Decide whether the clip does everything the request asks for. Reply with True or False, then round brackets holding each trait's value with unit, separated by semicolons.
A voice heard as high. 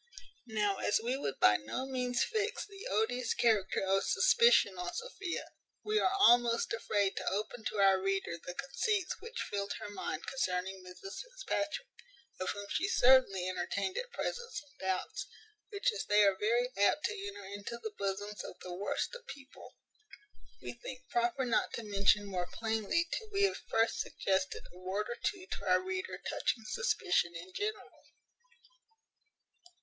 True (230 Hz)